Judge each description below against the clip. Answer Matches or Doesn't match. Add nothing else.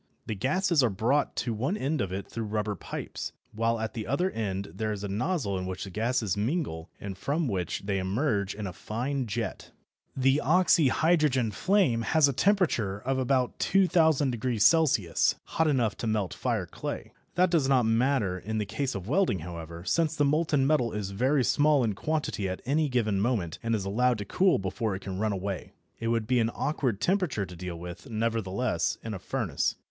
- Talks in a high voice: Doesn't match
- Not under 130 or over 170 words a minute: Doesn't match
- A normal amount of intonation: Doesn't match